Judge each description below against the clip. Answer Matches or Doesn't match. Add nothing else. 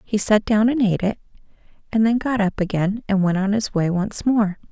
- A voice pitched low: Doesn't match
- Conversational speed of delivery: Doesn't match